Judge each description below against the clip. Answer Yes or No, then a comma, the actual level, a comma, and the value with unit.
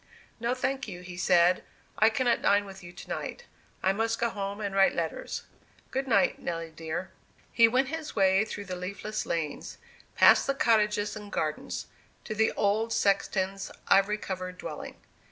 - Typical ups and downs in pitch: Yes, average, 3.6 semitones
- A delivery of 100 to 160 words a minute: No, average, 170 wpm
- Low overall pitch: No, high, 200 Hz